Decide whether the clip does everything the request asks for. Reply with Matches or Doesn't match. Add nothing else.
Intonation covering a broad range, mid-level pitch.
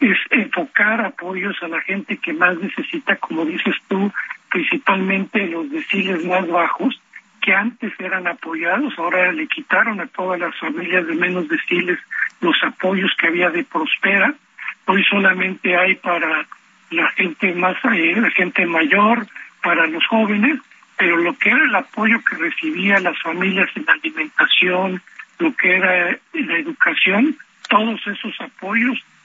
Doesn't match